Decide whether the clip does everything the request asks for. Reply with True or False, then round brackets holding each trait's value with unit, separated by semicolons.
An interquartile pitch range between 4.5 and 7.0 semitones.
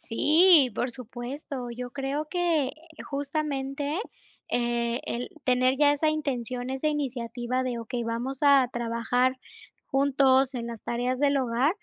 False (2.9 semitones)